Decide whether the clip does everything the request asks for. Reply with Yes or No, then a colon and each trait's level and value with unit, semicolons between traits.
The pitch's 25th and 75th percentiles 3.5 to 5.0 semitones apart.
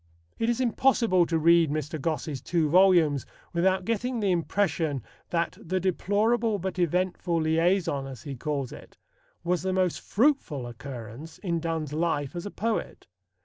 Yes: average, 3.9 semitones